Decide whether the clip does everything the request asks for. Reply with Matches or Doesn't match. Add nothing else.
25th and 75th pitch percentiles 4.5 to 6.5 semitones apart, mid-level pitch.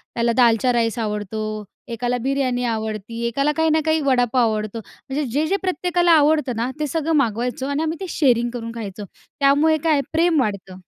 Doesn't match